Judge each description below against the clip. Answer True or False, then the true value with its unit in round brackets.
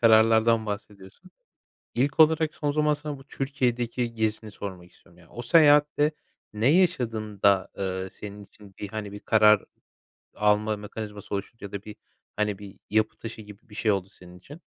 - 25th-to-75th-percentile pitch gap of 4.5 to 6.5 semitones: False (3.5 semitones)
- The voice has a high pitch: False (110 Hz)